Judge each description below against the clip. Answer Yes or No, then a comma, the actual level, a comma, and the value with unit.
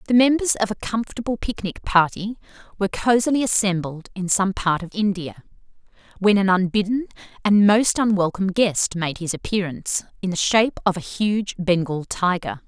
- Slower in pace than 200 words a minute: Yes, average, 160 wpm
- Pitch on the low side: No, high, 195 Hz